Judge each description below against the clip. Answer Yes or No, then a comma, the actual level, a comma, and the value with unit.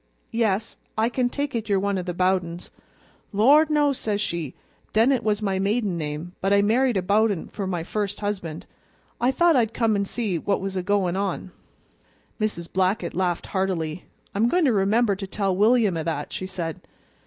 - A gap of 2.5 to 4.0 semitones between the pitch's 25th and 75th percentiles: Yes, average, 3.5 semitones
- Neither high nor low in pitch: No, high, 200 Hz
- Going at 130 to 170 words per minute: No, average, 190 wpm